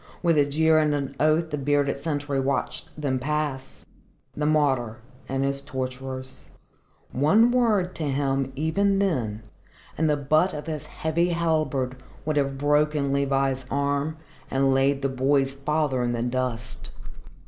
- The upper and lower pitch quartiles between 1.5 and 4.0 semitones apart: Yes, narrow, 2.6 semitones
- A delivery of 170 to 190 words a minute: No, average, 150 wpm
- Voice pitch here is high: No, medium, 140 Hz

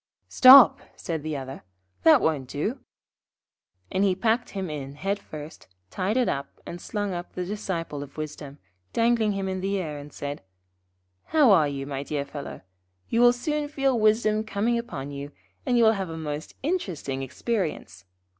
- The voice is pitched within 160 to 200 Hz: Yes, medium, 185 Hz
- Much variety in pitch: Yes, wide, 7.2 semitones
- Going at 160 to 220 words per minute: Yes, average, 170 wpm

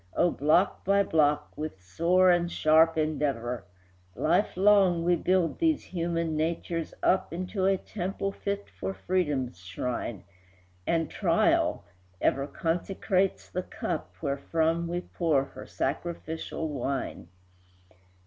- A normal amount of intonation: Yes, average, 3.7 semitones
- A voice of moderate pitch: Yes, medium, 165 Hz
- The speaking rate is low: Yes, slow, 115 wpm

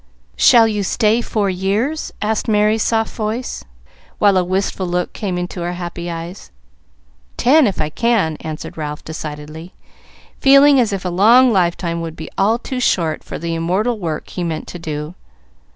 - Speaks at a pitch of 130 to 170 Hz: No, medium, 185 Hz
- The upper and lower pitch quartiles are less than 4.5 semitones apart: No, average, 5.0 semitones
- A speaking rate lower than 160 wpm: No, average, 170 wpm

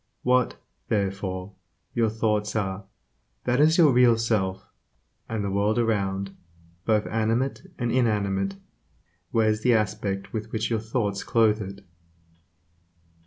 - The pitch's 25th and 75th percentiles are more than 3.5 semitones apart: No, narrow, 2.6 semitones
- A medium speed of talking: No, slow, 120 wpm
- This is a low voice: Yes, low, 110 Hz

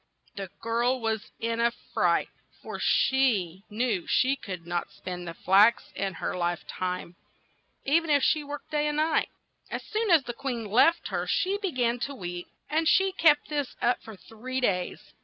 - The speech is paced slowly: No, average, 185 wpm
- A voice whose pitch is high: Yes, high, 240 Hz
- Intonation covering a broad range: Yes, wide, 7.3 semitones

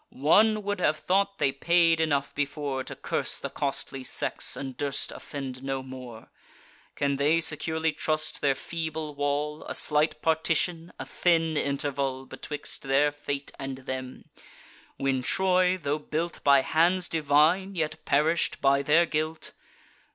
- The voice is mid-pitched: Yes, medium, 150 Hz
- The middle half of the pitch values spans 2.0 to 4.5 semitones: Yes, average, 2.8 semitones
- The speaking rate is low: No, average, 145 wpm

